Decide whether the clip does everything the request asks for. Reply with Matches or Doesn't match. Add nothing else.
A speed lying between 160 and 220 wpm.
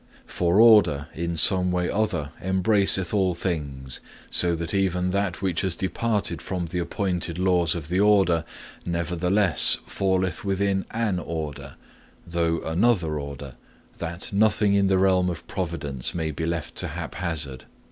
Doesn't match